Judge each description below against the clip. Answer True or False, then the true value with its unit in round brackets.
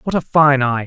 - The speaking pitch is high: False (140 Hz)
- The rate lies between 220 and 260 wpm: False (275 wpm)